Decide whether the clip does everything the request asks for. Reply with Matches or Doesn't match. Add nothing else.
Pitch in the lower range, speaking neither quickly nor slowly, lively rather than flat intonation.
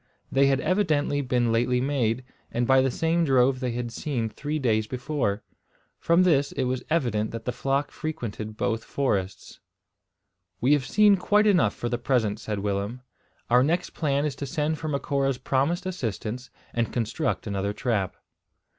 Doesn't match